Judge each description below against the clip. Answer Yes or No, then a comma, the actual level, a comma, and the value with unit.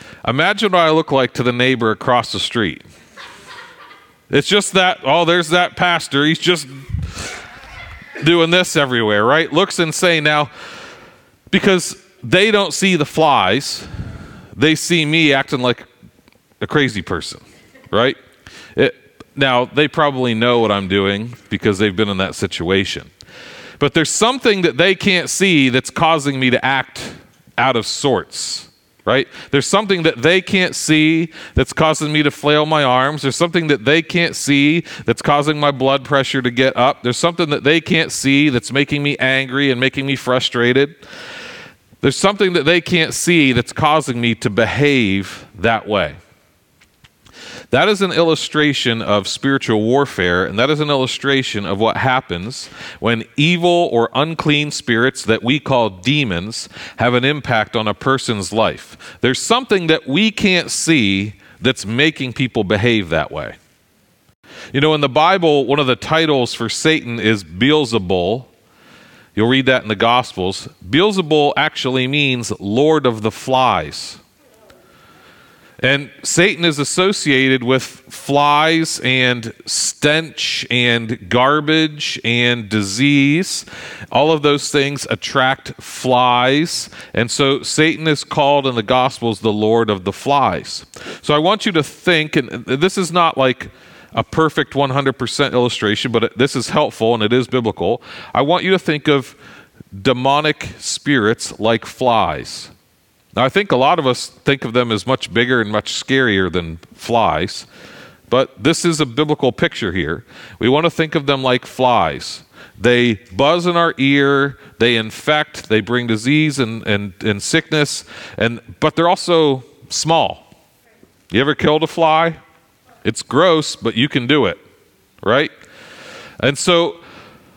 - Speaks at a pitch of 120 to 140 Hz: Yes, low, 135 Hz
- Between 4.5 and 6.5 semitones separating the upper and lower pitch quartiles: Yes, average, 4.8 semitones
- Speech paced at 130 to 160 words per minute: Yes, average, 155 wpm